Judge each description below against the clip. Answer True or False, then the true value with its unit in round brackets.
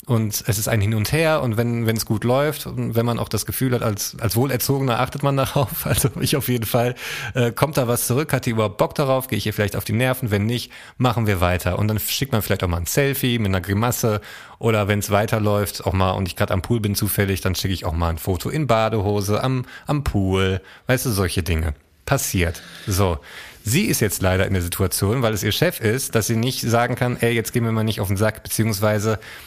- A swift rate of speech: True (250 wpm)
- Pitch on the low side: True (110 Hz)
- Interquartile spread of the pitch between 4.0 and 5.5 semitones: False (3.4 semitones)